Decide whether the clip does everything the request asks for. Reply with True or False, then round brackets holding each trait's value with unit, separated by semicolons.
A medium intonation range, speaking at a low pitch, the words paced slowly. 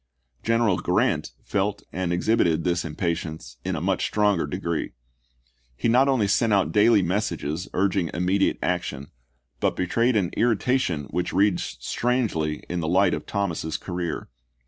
False (3.7 semitones; 95 Hz; 145 wpm)